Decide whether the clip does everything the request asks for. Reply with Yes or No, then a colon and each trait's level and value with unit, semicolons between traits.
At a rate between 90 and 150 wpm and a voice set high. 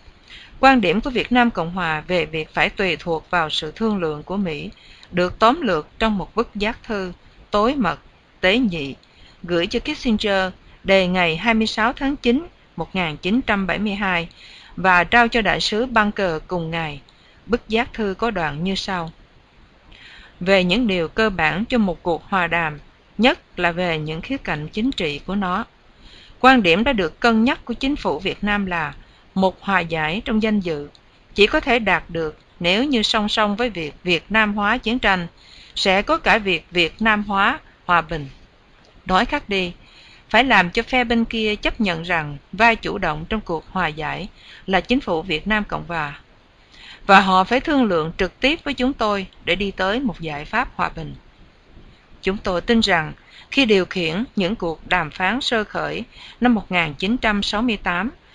No: average, 185 wpm; high, 195 Hz